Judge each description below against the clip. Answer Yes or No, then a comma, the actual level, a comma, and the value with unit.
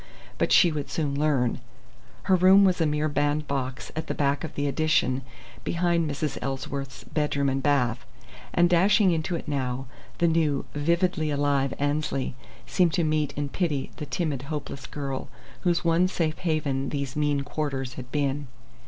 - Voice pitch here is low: No, medium, 145 Hz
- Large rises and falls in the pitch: No, average, 2.9 semitones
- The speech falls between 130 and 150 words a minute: No, average, 160 wpm